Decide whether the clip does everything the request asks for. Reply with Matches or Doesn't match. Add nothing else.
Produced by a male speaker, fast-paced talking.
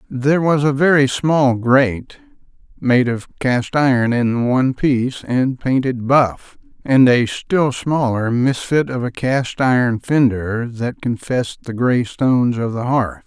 Doesn't match